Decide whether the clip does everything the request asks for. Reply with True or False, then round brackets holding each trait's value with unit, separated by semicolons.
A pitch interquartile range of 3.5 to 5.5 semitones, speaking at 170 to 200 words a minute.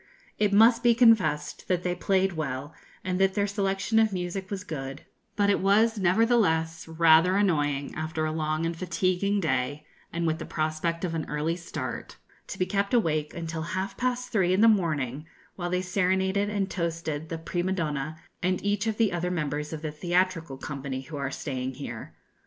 True (4.0 semitones; 185 wpm)